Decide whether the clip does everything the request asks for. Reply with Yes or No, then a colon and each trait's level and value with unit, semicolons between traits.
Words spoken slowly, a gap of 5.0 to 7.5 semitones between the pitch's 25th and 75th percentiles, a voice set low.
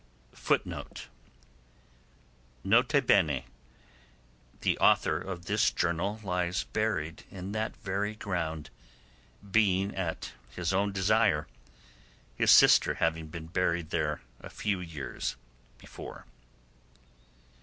No: slow, 90 wpm; average, 4.1 semitones; very low, 85 Hz